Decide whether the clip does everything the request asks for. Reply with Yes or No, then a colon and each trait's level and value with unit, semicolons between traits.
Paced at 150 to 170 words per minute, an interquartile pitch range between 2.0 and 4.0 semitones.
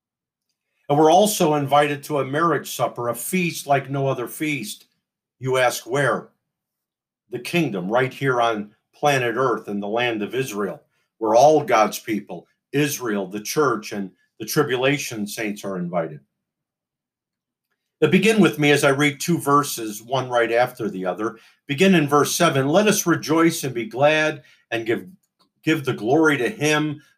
No: average, 160 wpm; average, 4.7 semitones